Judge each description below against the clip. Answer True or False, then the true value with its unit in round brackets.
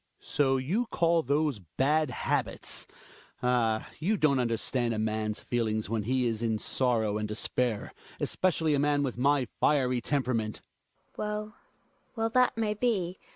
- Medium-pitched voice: False (130 Hz)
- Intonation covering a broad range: True (5.7 semitones)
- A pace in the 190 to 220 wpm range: False (160 wpm)